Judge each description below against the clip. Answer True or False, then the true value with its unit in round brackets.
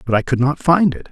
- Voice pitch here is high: False (140 Hz)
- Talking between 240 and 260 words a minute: False (320 wpm)